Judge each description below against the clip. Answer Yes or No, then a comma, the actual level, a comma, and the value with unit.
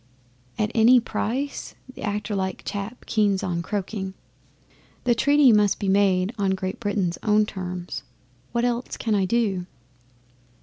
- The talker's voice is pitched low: No, high, 205 Hz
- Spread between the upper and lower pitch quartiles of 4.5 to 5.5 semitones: No, average, 3.3 semitones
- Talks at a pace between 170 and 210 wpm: No, average, 140 wpm